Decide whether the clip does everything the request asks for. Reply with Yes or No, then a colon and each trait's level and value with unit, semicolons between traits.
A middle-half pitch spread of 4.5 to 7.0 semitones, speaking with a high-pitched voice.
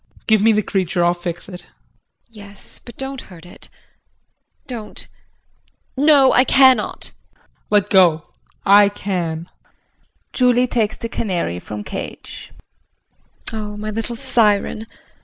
Yes: average, 4.8 semitones; high, 210 Hz